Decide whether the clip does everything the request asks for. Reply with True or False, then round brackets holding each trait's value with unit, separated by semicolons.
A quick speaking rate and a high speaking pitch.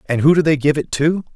False (310 wpm; 145 Hz)